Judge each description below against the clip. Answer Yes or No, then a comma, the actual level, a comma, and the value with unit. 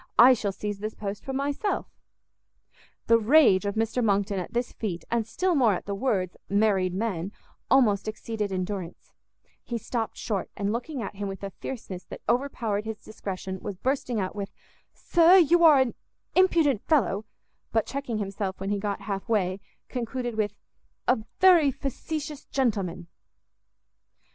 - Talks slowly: No, average, 160 wpm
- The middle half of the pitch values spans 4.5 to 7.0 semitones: Yes, average, 4.8 semitones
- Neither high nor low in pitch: No, high, 220 Hz